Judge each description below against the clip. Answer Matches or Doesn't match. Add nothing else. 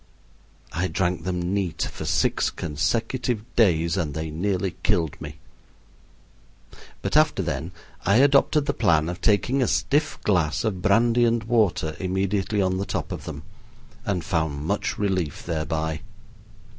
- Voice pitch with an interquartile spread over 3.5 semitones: Matches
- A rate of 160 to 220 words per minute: Doesn't match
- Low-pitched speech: Matches